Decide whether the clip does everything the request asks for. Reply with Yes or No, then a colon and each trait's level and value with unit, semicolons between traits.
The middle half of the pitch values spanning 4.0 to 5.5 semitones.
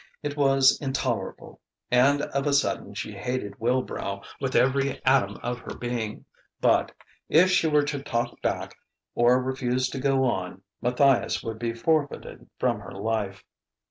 No: average, 2.9 semitones